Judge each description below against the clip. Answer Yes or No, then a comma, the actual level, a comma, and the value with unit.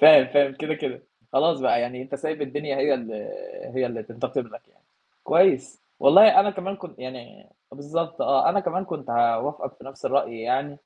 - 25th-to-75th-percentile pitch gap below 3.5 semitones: No, average, 4.3 semitones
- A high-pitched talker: No, medium, 145 Hz